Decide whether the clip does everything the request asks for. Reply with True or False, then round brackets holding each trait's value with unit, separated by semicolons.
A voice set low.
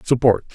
True (115 Hz)